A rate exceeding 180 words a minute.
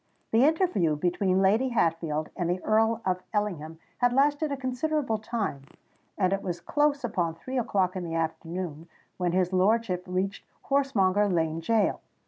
No: average, 155 wpm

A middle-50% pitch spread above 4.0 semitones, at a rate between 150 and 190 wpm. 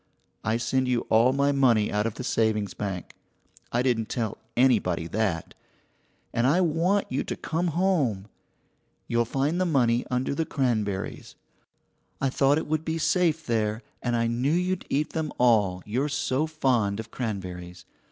Yes: wide, 5.4 semitones; average, 160 wpm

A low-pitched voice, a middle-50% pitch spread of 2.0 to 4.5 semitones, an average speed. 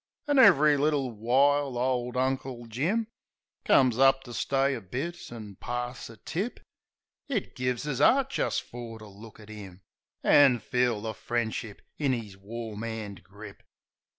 Yes: low, 125 Hz; average, 4.0 semitones; average, 150 wpm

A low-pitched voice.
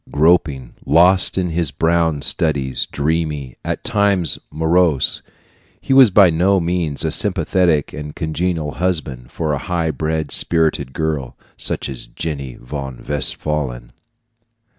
Yes: very low, 80 Hz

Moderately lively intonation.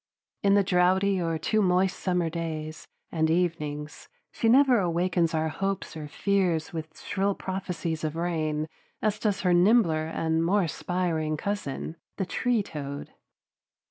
Yes: average, 3.6 semitones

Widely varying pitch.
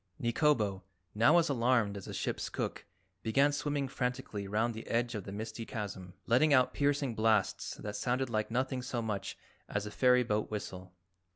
No: average, 3.6 semitones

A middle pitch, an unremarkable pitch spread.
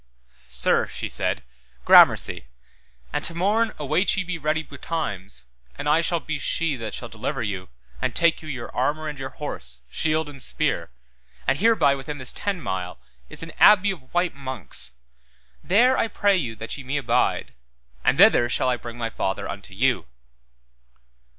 No: medium, 145 Hz; wide, 5.9 semitones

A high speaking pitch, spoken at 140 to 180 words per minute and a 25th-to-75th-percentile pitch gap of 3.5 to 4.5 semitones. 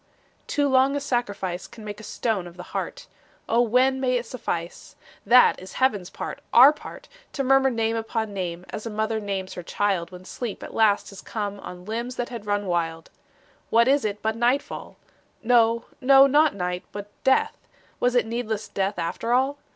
No: high, 225 Hz; average, 190 wpm; average, 4.2 semitones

